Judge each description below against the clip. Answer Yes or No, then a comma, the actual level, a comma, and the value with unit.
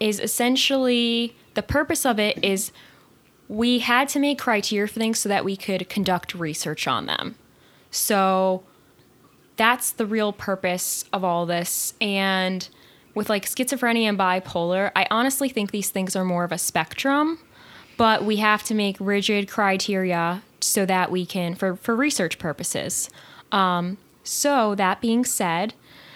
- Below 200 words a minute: Yes, average, 150 wpm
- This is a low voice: No, high, 205 Hz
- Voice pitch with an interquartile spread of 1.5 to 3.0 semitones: No, average, 3.8 semitones